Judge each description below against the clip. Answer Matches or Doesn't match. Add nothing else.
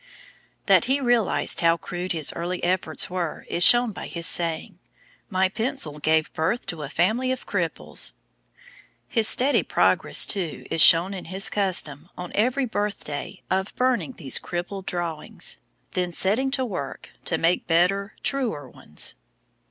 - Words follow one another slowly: Doesn't match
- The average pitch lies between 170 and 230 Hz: Matches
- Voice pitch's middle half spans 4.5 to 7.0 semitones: Matches